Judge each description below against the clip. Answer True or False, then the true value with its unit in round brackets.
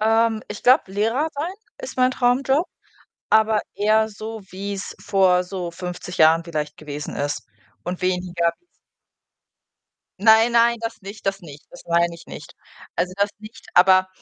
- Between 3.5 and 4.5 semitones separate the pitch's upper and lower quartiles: True (4.1 semitones)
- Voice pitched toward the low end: False (200 Hz)